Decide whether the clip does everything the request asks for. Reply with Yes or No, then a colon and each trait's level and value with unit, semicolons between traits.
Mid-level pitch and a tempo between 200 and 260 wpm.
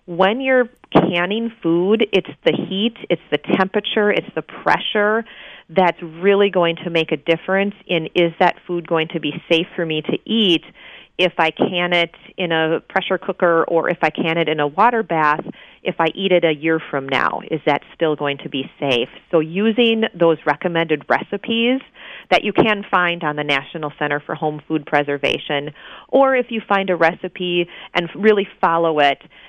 No: medium, 175 Hz; average, 185 wpm